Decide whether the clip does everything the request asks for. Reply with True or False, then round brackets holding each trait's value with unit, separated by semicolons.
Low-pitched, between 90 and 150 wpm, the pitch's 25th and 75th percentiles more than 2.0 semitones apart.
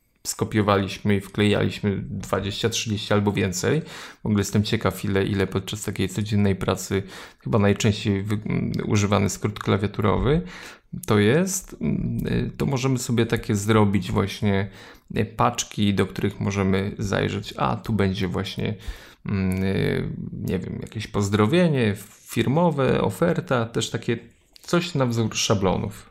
True (105 Hz; 115 wpm; 2.7 semitones)